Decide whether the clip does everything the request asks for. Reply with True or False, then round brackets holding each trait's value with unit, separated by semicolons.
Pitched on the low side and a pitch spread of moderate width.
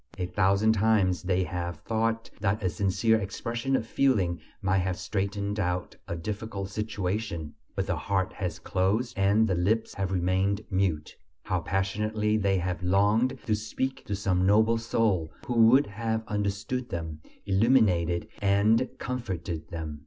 True (100 Hz; 3.3 semitones)